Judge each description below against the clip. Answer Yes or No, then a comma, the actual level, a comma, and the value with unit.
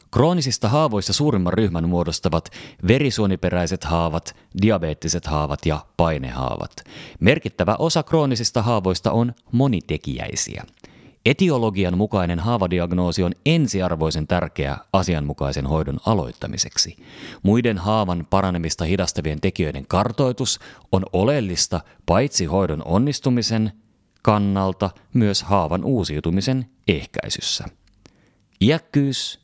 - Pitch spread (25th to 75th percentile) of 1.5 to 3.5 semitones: No, wide, 5.5 semitones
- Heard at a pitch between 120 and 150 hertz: No, very low, 95 Hz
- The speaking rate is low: Yes, slow, 90 wpm